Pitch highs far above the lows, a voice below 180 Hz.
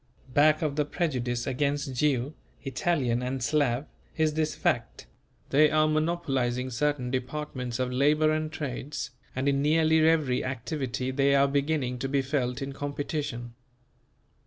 No: average, 3.1 semitones; medium, 140 Hz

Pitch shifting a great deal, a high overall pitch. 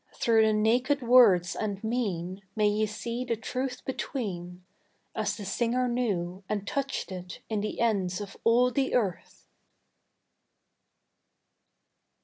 No: average, 4.1 semitones; high, 220 Hz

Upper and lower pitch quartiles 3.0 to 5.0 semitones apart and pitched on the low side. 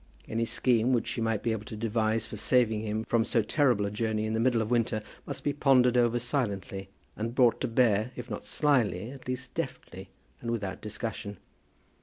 No: narrow, 2.5 semitones; low, 115 Hz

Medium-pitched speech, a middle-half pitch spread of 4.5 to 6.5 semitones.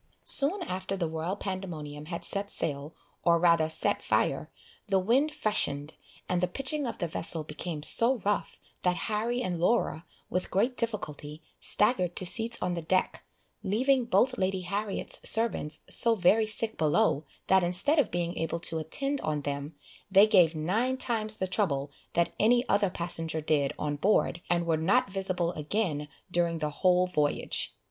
Yes: medium, 180 Hz; average, 5.1 semitones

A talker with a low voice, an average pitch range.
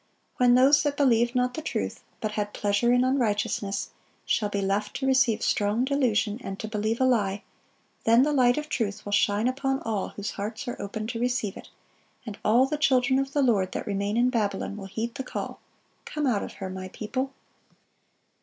No: high, 230 Hz; average, 4.0 semitones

